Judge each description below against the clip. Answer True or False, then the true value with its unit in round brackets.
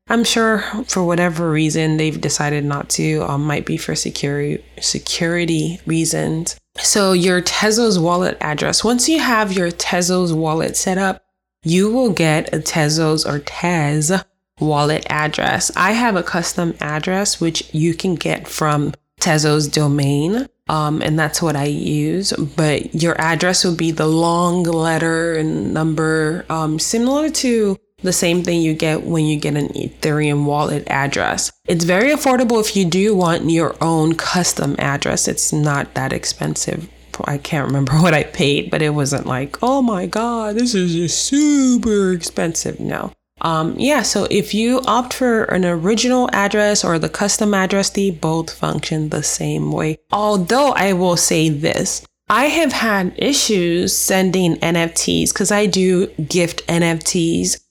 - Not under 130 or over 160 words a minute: True (155 wpm)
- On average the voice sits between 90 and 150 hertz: False (170 Hz)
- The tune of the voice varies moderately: True (4.4 semitones)